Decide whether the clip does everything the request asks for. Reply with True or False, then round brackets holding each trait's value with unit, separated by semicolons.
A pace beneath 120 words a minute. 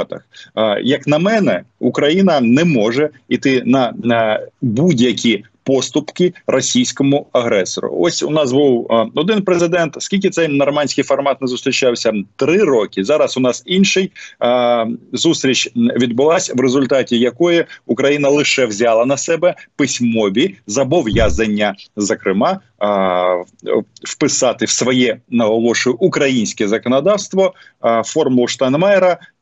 True (110 wpm)